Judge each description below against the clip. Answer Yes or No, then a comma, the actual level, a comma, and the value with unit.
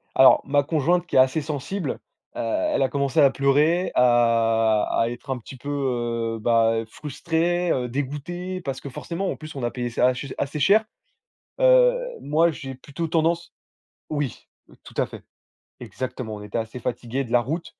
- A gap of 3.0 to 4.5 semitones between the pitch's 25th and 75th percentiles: No, average, 5.0 semitones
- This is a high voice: No, low, 135 Hz